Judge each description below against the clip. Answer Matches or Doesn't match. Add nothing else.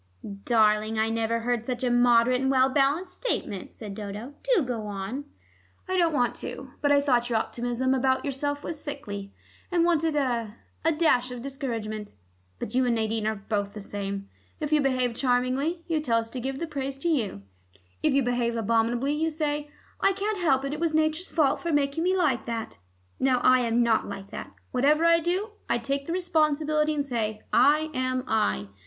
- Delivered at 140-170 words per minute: Doesn't match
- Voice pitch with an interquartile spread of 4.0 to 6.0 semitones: Matches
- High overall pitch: Matches